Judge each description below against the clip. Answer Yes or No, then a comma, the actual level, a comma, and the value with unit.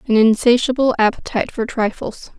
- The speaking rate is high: No, slow, 125 wpm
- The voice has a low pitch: No, high, 230 Hz